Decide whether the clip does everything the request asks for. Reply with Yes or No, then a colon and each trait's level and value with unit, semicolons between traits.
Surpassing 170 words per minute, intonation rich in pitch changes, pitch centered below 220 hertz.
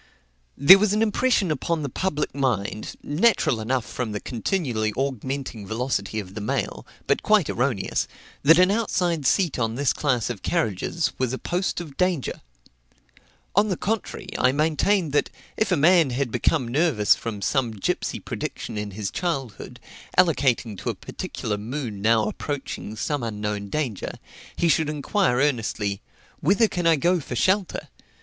No: average, 160 wpm; wide, 7.4 semitones; medium, 140 Hz